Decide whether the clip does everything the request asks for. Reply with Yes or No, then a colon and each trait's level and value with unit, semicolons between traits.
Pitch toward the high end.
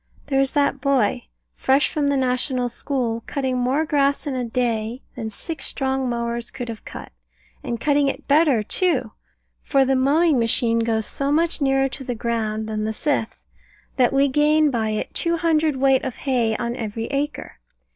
Yes: very high, 260 Hz